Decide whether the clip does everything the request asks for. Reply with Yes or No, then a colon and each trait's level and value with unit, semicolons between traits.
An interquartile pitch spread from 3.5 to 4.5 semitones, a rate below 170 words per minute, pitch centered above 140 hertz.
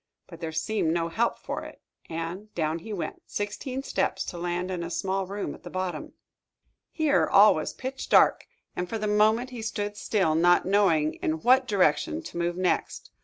No: average, 4.1 semitones; average, 190 wpm; medium, 185 Hz